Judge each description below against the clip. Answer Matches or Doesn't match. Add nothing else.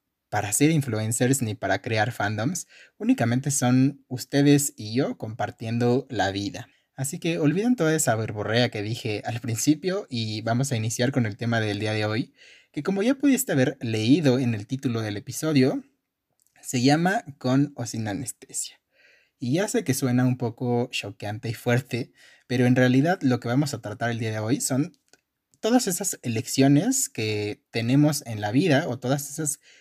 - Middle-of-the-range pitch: Doesn't match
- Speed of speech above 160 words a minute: Matches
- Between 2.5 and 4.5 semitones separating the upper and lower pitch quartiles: Matches